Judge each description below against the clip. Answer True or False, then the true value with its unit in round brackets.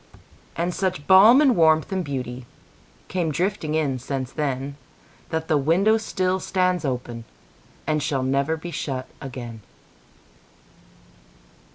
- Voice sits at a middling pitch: True (155 Hz)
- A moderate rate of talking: False (105 wpm)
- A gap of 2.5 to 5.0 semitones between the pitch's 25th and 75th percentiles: False (5.6 semitones)